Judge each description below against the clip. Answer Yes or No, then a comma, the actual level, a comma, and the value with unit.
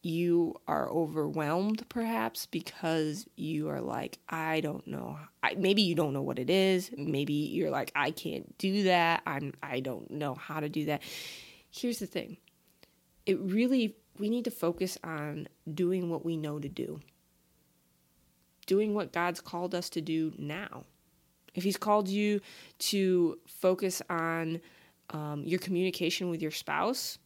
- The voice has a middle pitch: Yes, medium, 170 Hz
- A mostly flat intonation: No, average, 4.0 semitones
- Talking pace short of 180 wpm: Yes, average, 155 wpm